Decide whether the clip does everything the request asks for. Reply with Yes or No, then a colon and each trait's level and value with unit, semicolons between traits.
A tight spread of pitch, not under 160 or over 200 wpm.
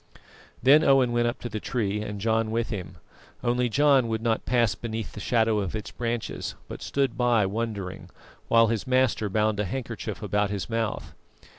Yes: narrow, 2.3 semitones; average, 180 wpm